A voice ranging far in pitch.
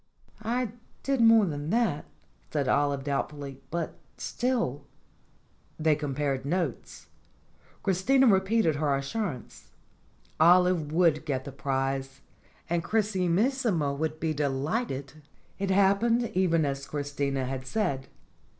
Yes: wide, 6.0 semitones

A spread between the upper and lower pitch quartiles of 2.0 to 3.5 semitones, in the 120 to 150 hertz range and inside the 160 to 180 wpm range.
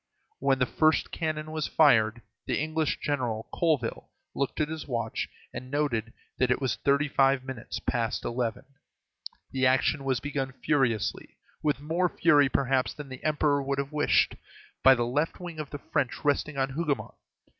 Yes: average, 2.8 semitones; medium, 140 Hz; average, 165 wpm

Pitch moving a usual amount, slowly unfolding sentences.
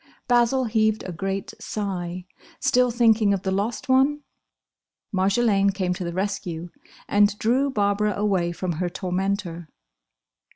Yes: average, 3.3 semitones; slow, 130 wpm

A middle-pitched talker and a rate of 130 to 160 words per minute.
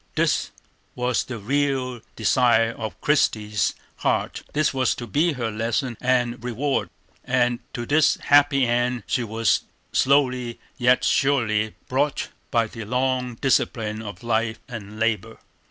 No: low, 120 Hz; slow, 135 wpm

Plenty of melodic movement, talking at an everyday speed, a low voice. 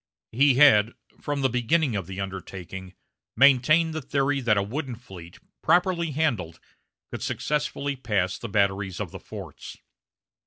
Yes: wide, 6.8 semitones; average, 145 wpm; low, 125 Hz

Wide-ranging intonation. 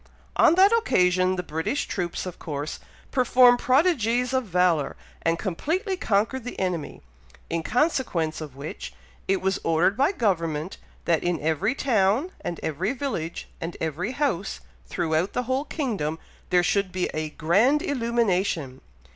Yes: wide, 7.3 semitones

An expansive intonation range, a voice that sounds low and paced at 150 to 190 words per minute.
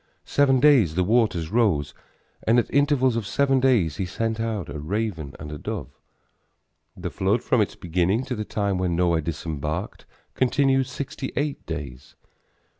Yes: wide, 7.5 semitones; low, 105 Hz; average, 160 wpm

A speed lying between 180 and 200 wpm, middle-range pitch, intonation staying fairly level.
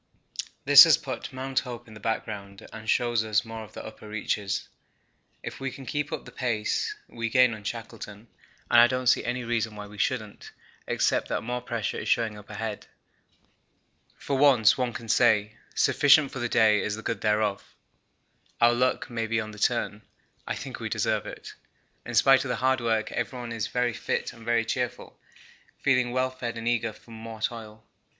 No: average, 190 wpm; low, 115 Hz; narrow, 2.3 semitones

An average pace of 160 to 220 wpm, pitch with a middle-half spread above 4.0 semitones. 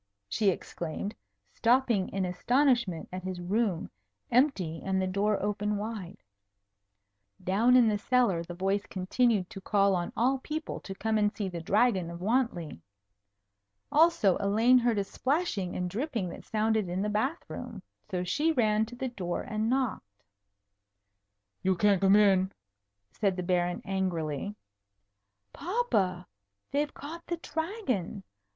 No: average, 145 wpm; average, 4.9 semitones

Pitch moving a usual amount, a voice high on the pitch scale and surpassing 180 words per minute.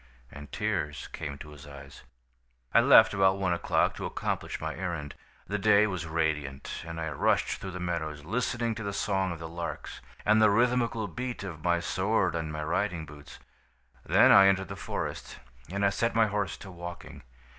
No: average, 4.5 semitones; very low, 90 Hz; average, 190 wpm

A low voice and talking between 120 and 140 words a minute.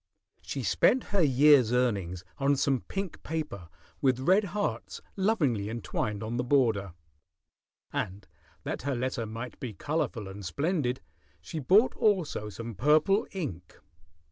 Yes: low, 130 Hz; slow, 135 wpm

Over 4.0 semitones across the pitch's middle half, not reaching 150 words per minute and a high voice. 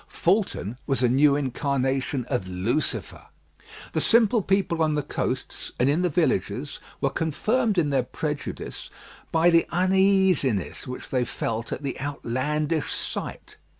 No: wide, 5.4 semitones; average, 140 wpm; medium, 145 Hz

